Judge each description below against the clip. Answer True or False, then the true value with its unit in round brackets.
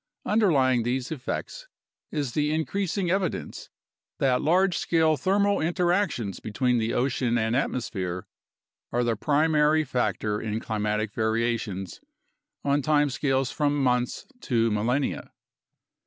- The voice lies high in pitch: False (130 Hz)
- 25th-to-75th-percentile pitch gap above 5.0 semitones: True (5.4 semitones)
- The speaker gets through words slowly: True (120 wpm)